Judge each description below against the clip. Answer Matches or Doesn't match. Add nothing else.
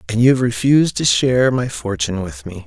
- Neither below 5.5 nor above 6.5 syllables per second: Matches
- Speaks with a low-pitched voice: Matches